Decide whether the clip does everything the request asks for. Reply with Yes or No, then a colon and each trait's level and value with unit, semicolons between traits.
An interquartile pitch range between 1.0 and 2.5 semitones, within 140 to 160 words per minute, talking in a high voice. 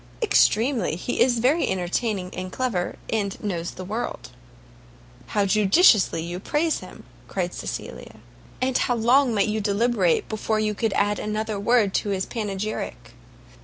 No: average, 3.9 semitones; average, 150 wpm; high, 215 Hz